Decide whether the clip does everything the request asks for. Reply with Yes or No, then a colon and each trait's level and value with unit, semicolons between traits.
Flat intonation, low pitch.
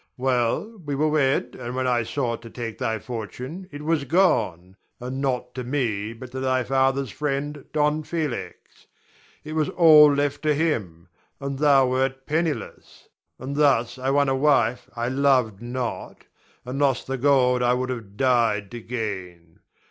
No: average, 3.3 semitones; low, 130 Hz